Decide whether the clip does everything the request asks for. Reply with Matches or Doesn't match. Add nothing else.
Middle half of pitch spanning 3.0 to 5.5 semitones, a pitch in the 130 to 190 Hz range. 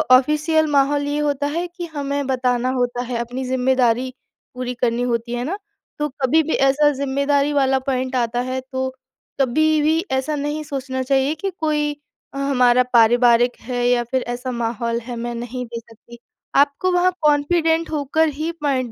Doesn't match